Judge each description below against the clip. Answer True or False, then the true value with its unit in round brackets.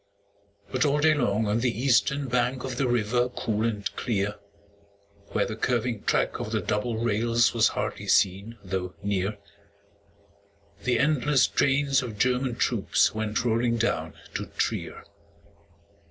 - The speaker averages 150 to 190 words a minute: False (140 wpm)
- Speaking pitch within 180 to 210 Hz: False (120 Hz)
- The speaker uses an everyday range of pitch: True (3.0 semitones)